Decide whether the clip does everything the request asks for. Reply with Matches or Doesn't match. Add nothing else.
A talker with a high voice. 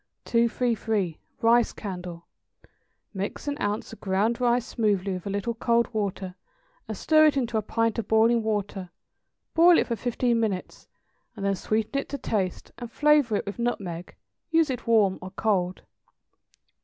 Matches